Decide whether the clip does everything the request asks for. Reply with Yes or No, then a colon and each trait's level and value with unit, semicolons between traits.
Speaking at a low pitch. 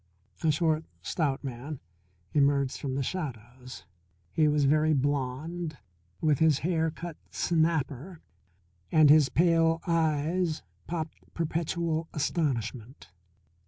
No: medium, 155 Hz